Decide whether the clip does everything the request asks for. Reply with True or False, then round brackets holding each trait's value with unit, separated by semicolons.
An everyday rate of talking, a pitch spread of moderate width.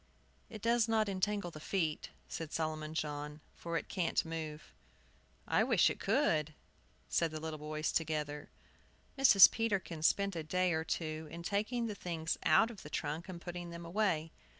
True (170 wpm; 4.2 semitones)